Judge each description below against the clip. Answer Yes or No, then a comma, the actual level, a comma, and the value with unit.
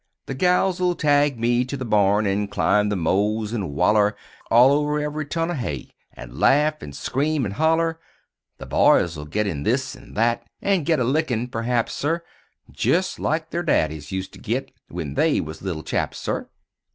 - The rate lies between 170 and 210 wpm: Yes, average, 190 wpm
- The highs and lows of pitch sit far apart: Yes, wide, 7.4 semitones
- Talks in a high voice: No, low, 120 Hz